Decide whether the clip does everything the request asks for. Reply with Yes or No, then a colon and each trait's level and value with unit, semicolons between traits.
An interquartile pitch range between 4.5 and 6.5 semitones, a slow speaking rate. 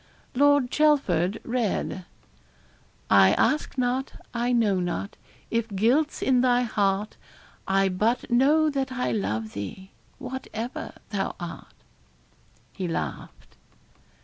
Yes: average, 5.1 semitones; slow, 110 wpm